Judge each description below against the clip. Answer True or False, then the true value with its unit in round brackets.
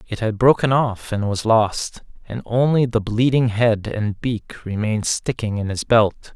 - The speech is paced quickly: False (180 wpm)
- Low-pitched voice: True (110 Hz)